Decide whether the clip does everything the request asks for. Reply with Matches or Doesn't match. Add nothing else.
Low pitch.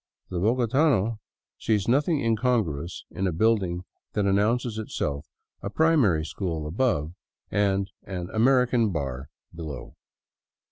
Matches